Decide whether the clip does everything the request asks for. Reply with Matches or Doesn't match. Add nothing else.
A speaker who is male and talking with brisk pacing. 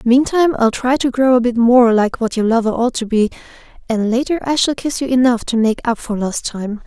Doesn't match